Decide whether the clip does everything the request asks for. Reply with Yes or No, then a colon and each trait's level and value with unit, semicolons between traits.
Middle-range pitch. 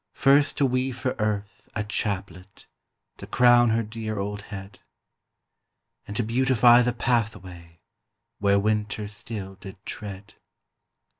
No: low, 105 Hz